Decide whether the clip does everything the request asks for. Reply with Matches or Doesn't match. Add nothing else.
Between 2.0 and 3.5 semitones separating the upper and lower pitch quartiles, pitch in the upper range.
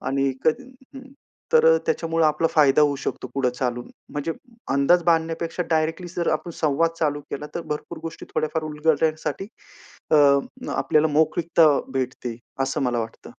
Doesn't match